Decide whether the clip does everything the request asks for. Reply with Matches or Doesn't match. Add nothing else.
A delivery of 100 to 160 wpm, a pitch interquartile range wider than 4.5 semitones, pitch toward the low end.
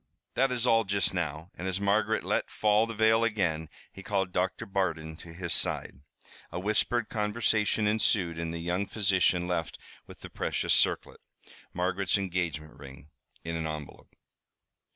Doesn't match